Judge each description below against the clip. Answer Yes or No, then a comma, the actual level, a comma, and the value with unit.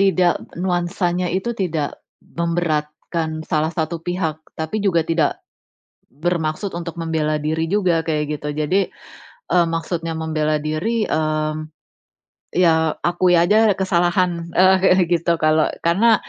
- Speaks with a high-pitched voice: No, medium, 170 Hz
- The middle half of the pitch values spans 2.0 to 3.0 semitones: Yes, narrow, 2.4 semitones